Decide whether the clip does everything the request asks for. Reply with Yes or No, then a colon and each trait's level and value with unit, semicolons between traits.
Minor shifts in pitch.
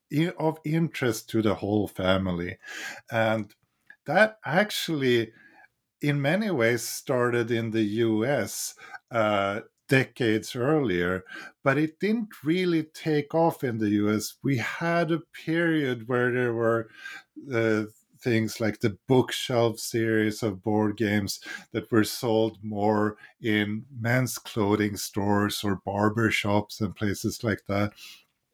No: average, 4.8 semitones